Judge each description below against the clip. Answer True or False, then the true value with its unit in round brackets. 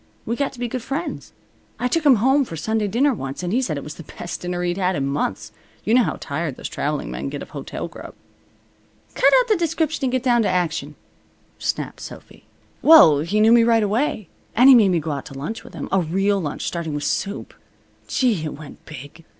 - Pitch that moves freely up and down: True (8.1 semitones)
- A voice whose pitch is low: False (195 Hz)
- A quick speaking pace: True (230 wpm)